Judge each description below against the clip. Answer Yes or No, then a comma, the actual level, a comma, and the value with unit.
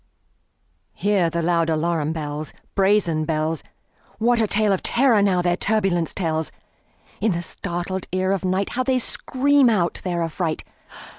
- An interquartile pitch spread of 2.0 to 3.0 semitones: No, average, 4.0 semitones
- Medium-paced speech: No, slow, 130 wpm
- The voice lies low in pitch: No, medium, 180 Hz